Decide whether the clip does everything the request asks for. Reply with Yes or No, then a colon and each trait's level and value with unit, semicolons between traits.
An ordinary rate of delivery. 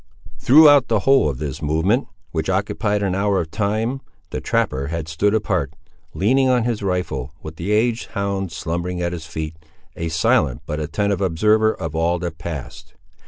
Yes: average, 170 wpm